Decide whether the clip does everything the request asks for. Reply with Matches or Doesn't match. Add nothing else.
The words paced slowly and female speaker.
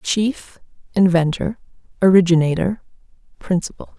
Matches